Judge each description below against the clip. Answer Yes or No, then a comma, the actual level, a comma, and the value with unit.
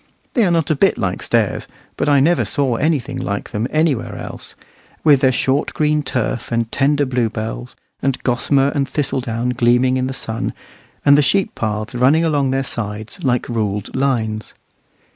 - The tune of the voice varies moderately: Yes, average, 3.7 semitones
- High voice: No, low, 130 Hz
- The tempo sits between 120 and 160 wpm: No, average, 175 wpm